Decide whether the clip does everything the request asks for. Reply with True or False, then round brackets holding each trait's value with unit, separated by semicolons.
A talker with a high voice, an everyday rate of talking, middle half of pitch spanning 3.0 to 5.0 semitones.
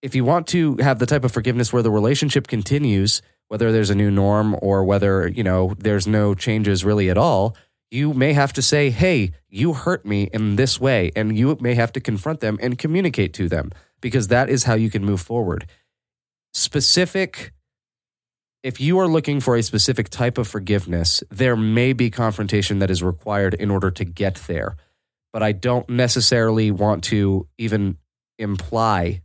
False (110 Hz; 185 wpm; 4.3 semitones)